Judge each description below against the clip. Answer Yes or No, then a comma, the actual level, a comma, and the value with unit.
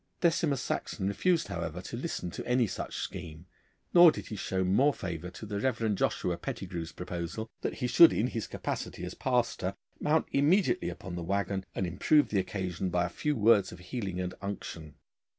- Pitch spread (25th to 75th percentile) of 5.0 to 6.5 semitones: Yes, wide, 5.6 semitones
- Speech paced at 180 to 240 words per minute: Yes, average, 185 wpm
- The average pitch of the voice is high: No, low, 100 Hz